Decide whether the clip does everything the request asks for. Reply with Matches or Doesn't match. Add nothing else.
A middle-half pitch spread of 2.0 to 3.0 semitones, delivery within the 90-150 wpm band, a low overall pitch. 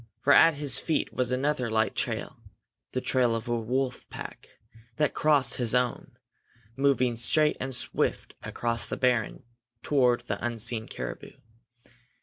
Matches